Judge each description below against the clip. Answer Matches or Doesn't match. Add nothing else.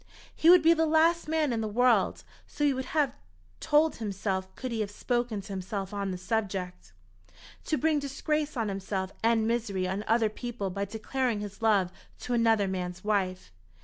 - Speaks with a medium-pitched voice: Doesn't match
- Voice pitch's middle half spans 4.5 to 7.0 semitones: Matches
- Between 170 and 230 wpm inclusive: Matches